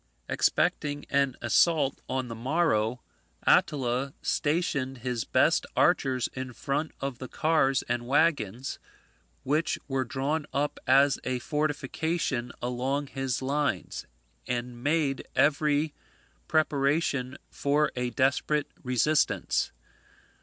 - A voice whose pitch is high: No, low, 135 Hz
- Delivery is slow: Yes, slow, 105 wpm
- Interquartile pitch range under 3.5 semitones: Yes, average, 2.8 semitones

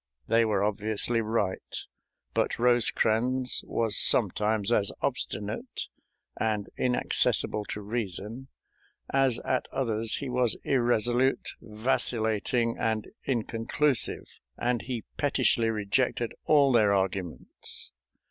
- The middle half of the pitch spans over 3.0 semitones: No, average, 2.7 semitones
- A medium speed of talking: No, slow, 100 wpm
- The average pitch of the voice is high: No, low, 115 Hz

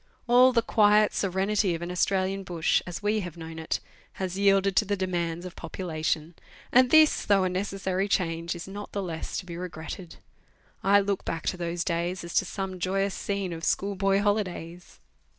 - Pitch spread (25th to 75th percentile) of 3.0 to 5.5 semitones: No, narrow, 2.5 semitones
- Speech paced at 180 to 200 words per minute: Yes, average, 185 wpm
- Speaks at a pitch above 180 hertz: Yes, high, 190 Hz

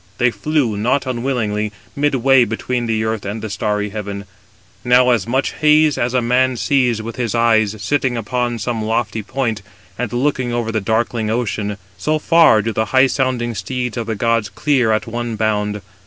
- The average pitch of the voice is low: Yes, low, 115 Hz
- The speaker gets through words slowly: No, average, 185 wpm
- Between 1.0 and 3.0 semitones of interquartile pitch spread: Yes, average, 2.7 semitones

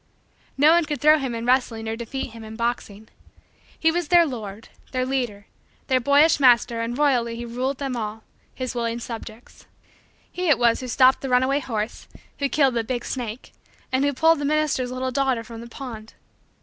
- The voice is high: Yes, very high, 250 Hz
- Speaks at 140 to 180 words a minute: No, average, 190 wpm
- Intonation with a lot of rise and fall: No, average, 3.2 semitones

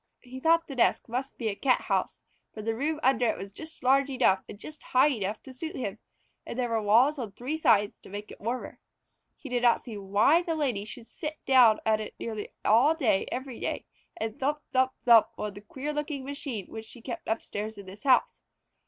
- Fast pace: Yes, fast, 215 wpm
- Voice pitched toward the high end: Yes, high, 245 Hz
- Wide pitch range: No, average, 4.3 semitones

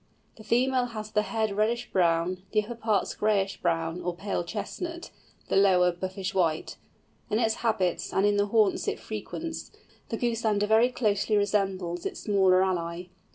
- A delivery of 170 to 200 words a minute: No, average, 160 wpm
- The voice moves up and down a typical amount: Yes, average, 3.1 semitones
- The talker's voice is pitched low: No, high, 205 Hz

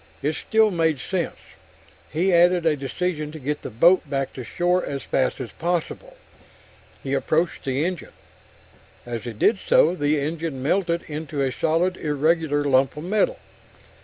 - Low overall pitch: No, medium, 155 Hz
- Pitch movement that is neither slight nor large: Yes, average, 4.0 semitones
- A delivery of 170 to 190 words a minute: No, average, 160 wpm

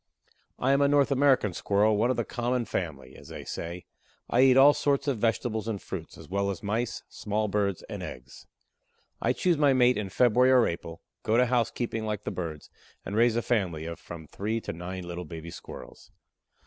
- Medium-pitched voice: No, low, 110 Hz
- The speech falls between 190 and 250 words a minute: Yes, average, 200 wpm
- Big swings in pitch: Yes, wide, 5.7 semitones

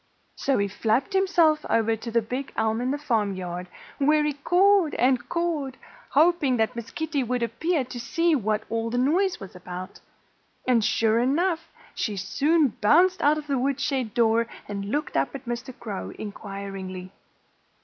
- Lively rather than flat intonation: Yes, wide, 5.7 semitones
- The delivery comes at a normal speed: Yes, average, 170 wpm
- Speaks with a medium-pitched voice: No, very high, 250 Hz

